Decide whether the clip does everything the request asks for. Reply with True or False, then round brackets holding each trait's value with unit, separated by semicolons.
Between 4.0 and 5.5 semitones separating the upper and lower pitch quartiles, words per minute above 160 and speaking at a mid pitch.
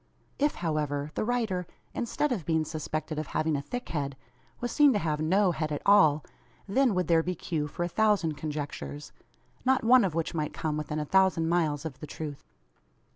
True (4.8 semitones; 195 wpm; 160 Hz)